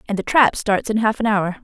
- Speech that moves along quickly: Yes, fast, 295 wpm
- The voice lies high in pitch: Yes, high, 210 Hz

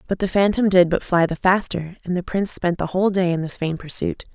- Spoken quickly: Yes, fast, 260 wpm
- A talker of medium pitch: Yes, medium, 180 Hz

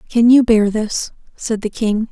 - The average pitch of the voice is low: No, high, 220 Hz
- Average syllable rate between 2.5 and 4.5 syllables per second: Yes, 4.1 syllables/s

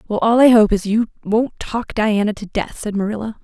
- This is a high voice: Yes, high, 215 Hz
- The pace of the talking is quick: Yes, fast, 225 wpm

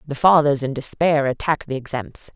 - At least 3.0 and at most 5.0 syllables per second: No, 5.4 syllables/s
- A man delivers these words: No, female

